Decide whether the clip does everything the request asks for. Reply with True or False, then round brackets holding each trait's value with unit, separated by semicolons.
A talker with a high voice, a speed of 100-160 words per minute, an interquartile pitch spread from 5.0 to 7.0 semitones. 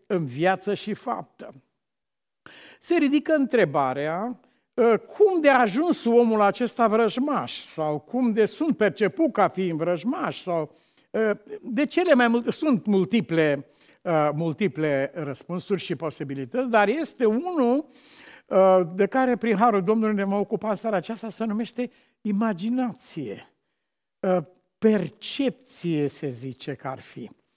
True (215 Hz; 120 wpm; 5.6 semitones)